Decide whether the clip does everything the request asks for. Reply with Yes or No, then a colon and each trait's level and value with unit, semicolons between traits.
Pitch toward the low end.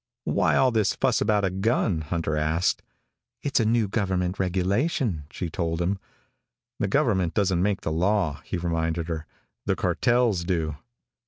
Yes: very low, 90 Hz